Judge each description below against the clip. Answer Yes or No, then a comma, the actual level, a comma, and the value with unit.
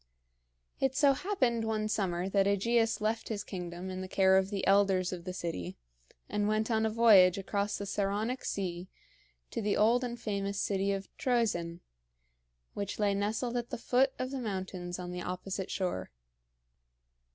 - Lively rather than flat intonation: No, average, 3.2 semitones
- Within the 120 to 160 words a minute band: No, average, 170 wpm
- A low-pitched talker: No, high, 200 Hz